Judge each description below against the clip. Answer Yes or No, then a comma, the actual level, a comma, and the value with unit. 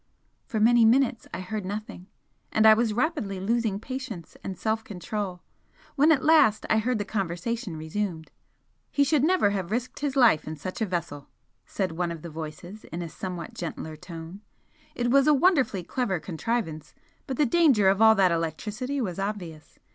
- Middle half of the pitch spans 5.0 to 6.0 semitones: Yes, wide, 5.5 semitones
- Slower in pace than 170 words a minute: No, average, 180 wpm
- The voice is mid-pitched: No, high, 210 Hz